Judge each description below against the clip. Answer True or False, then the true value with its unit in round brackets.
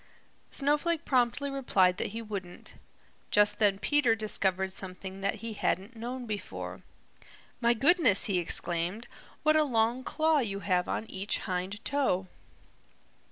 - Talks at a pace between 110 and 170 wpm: True (135 wpm)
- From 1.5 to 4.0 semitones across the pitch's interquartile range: False (5.3 semitones)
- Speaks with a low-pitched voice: False (215 Hz)